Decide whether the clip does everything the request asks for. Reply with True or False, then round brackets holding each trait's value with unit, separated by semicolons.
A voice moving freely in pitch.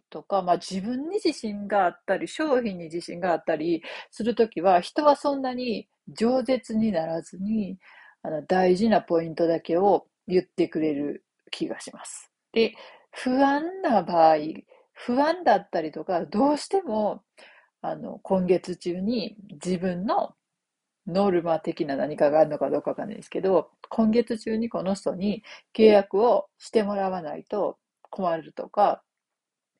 True (5.7 semitones)